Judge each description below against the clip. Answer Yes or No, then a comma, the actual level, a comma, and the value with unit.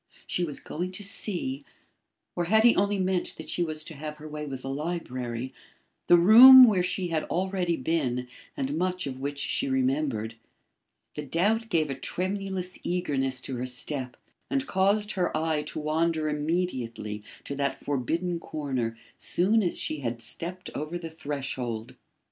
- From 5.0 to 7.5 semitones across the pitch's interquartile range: Yes, average, 5.3 semitones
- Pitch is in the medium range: Yes, medium, 155 Hz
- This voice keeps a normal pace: Yes, average, 165 wpm